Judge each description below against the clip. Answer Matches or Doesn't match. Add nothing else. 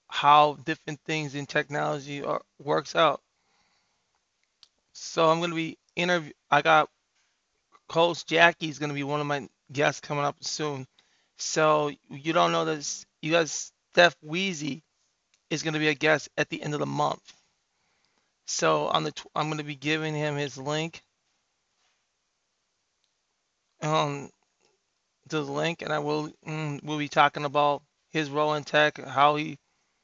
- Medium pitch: Matches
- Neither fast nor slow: Matches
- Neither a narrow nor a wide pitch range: Doesn't match